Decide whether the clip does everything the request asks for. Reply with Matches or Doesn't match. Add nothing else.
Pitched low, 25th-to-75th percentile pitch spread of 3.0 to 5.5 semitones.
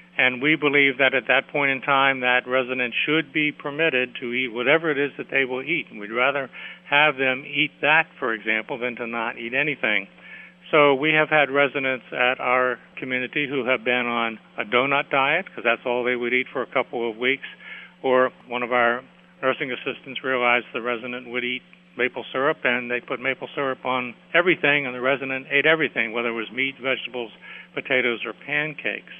Doesn't match